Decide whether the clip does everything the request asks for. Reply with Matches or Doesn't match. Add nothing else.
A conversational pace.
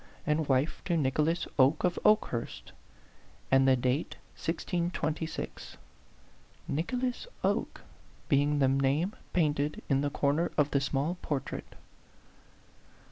Doesn't match